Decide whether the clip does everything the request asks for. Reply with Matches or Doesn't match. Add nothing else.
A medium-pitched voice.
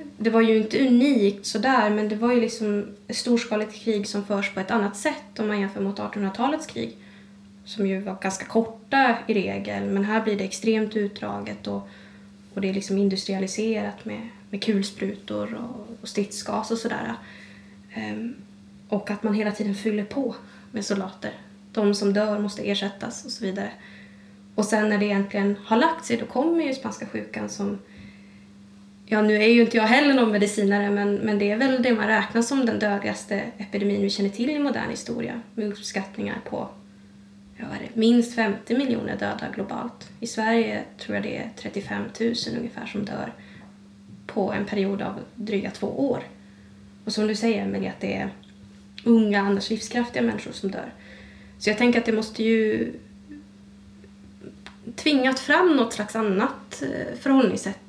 Doesn't match